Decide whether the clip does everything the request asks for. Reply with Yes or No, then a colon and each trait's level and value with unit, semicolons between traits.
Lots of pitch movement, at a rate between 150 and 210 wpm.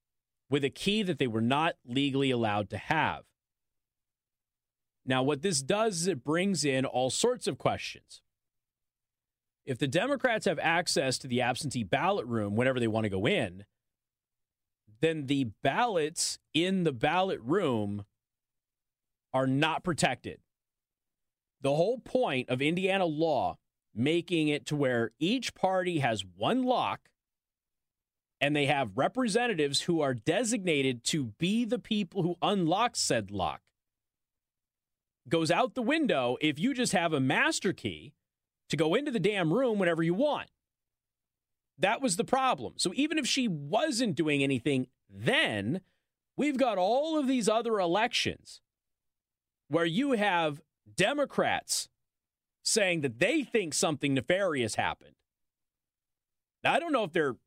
No: wide, 7.8 semitones; average, 140 wpm